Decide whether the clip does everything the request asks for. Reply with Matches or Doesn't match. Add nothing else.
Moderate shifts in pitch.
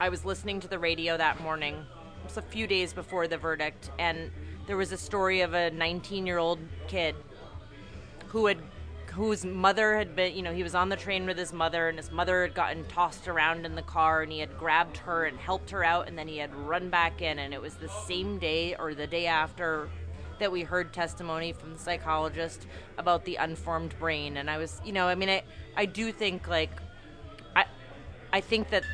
Matches